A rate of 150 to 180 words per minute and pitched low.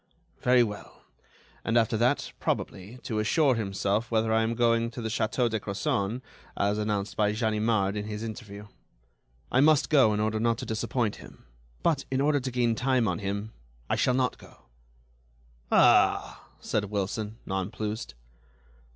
Yes: average, 160 wpm; low, 110 Hz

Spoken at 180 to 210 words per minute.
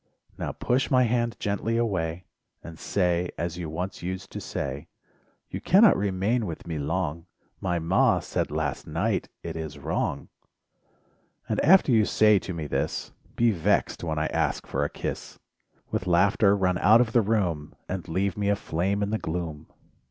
No: average, 170 wpm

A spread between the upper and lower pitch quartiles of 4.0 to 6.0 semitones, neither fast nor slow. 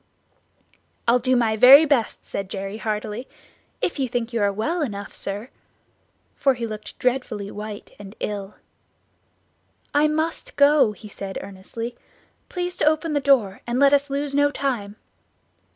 Yes: average, 5.3 semitones; average, 150 wpm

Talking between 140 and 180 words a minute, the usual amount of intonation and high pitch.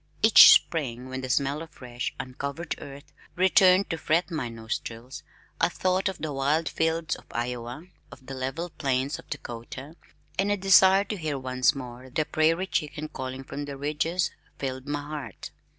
No: average, 170 wpm; average, 4.1 semitones; medium, 145 Hz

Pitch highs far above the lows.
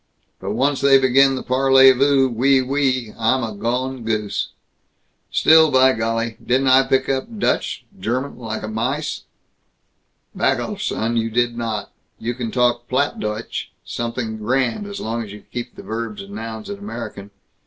No: average, 2.9 semitones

